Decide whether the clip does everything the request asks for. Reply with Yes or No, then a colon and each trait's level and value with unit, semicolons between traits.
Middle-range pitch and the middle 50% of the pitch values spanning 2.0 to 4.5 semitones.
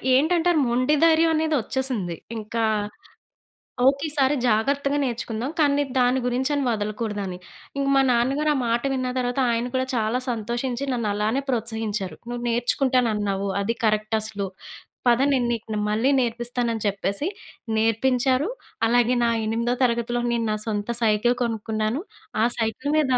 No: high, 240 Hz; average, 3.2 semitones